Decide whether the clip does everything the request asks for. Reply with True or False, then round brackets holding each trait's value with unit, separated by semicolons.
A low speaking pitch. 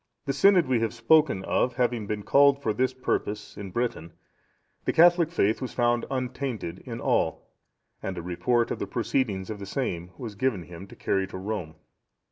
True (115 Hz)